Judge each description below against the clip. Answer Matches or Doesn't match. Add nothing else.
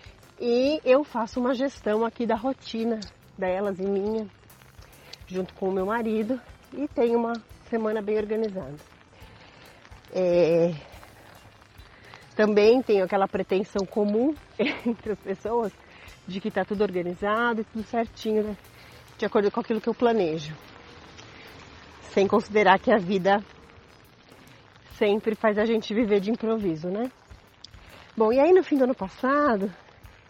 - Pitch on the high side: Matches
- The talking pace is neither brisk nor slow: Matches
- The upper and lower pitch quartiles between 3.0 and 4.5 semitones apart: Matches